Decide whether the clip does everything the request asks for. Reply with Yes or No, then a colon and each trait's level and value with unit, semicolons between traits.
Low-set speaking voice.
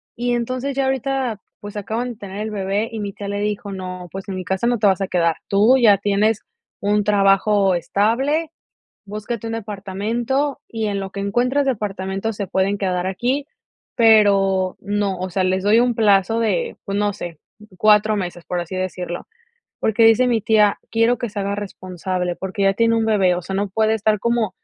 No: high, 205 Hz